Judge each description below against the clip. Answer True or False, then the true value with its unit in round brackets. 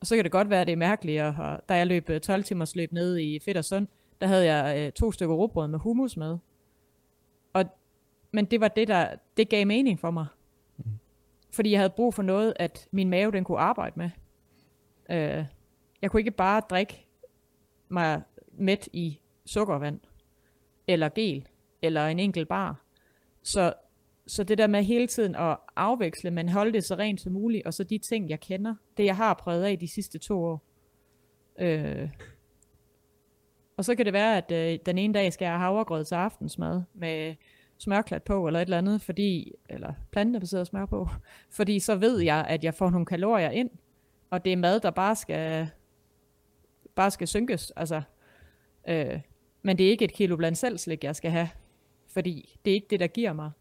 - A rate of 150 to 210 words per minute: True (195 wpm)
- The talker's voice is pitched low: False (185 Hz)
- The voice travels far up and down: False (4.1 semitones)